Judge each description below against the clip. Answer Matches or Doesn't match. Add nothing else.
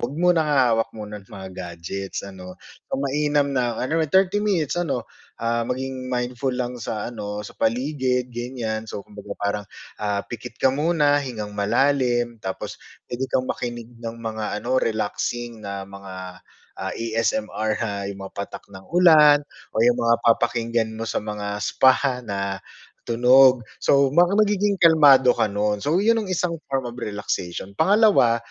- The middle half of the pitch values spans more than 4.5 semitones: Matches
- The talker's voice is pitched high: Doesn't match